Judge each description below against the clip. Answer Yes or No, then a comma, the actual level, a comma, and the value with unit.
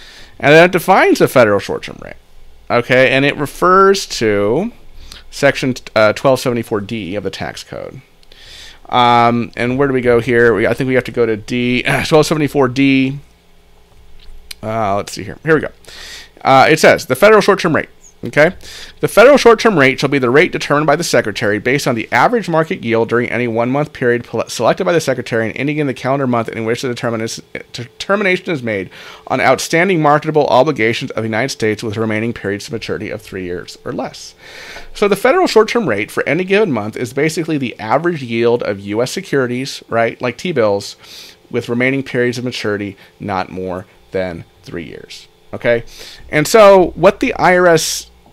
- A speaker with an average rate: Yes, average, 185 wpm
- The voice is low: Yes, low, 125 Hz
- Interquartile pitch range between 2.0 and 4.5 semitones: No, average, 5.2 semitones